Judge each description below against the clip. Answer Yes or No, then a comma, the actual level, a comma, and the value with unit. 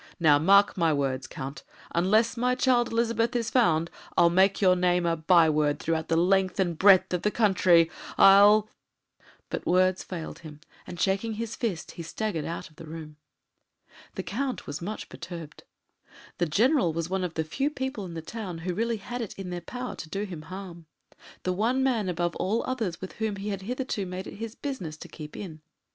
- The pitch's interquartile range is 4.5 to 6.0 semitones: Yes, average, 4.8 semitones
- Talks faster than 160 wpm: Yes, average, 200 wpm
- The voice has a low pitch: No, medium, 185 Hz